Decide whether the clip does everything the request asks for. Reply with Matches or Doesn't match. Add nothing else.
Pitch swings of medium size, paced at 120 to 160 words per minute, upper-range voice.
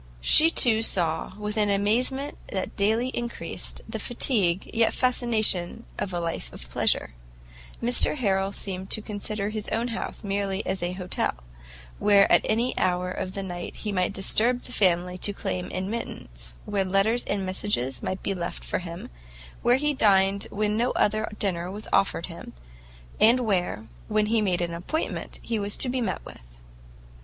Doesn't match